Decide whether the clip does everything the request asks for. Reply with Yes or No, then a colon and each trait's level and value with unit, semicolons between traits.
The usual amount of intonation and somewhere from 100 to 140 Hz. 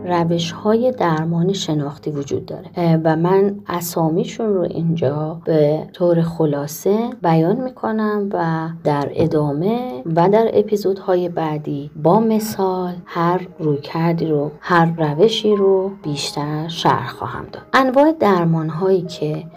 No: average, 3.7 semitones; medium, 170 Hz